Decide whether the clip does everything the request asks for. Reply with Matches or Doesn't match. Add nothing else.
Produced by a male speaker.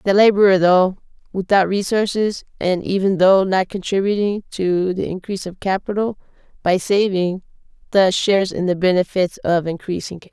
Doesn't match